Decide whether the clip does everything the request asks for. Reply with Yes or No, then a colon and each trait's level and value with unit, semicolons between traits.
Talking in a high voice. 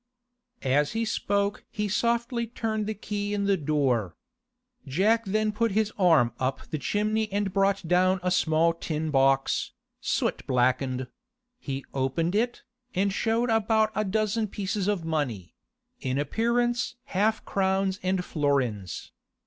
Yes: high, 195 Hz